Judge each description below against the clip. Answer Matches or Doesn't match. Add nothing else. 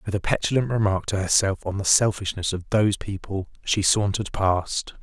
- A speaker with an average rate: Matches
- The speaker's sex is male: Matches